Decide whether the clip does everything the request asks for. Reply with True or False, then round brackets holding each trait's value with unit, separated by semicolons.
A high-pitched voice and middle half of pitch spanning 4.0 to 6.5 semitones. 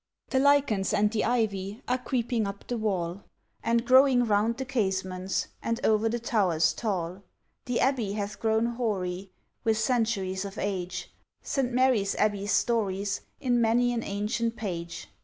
False (220 Hz; 3.4 semitones)